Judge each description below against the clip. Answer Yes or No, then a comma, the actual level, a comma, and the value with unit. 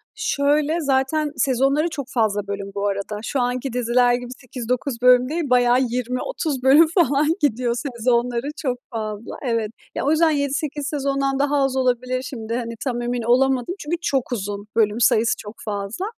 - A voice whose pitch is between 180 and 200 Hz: No, very high, 250 Hz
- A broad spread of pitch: No, average, 3.2 semitones